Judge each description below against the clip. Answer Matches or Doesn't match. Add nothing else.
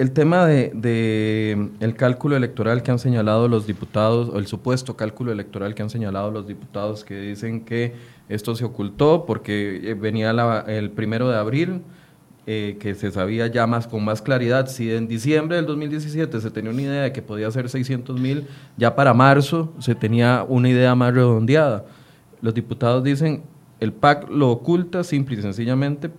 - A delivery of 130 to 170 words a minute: Doesn't match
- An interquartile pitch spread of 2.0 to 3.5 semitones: Doesn't match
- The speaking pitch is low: Matches